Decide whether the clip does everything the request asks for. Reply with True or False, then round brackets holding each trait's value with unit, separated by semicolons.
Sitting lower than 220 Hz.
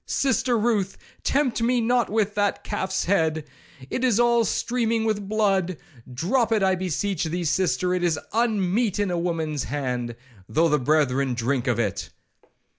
True (190 Hz)